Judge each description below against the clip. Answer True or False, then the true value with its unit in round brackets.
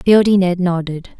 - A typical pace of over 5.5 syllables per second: False (5.1 syllables/s)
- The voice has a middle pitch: True (180 Hz)